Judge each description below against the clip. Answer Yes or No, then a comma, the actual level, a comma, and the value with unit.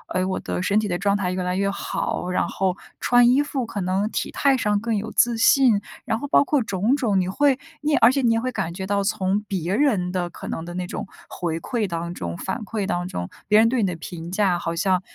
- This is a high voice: Yes, high, 200 Hz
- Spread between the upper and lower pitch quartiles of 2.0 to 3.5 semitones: No, average, 4.4 semitones